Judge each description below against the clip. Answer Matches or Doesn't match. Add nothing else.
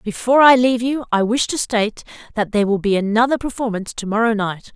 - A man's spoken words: Doesn't match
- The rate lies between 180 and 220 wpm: Matches